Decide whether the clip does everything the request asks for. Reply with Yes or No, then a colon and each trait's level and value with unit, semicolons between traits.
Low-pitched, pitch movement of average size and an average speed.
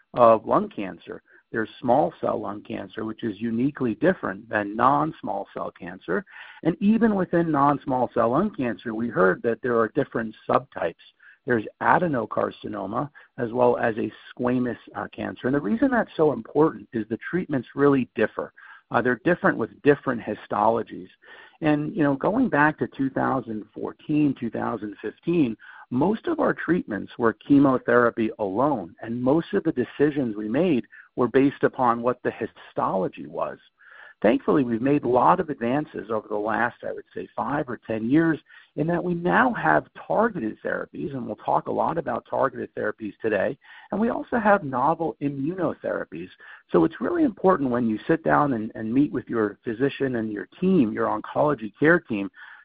No: low, 130 Hz; wide, 5.7 semitones; average, 170 wpm